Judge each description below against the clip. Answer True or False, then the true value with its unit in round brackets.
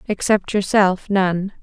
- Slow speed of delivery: True (110 wpm)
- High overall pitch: True (195 Hz)